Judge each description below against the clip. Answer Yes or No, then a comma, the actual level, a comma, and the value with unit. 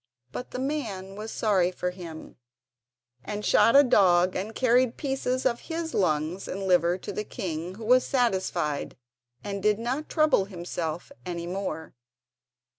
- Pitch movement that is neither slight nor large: No, wide, 5.7 semitones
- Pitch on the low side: No, high, 200 Hz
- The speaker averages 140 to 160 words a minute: Yes, average, 150 wpm